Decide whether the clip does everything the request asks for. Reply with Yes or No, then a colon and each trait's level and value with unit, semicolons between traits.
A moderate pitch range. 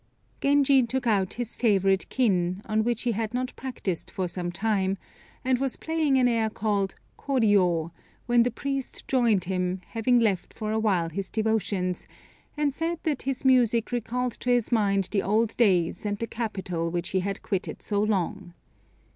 Yes: average, 4.3 semitones